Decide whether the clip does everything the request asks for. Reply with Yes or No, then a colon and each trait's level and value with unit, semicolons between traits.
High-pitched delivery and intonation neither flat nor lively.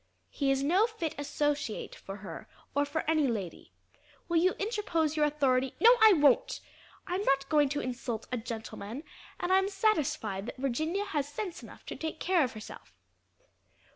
No: very high, 295 Hz; wide, 5.7 semitones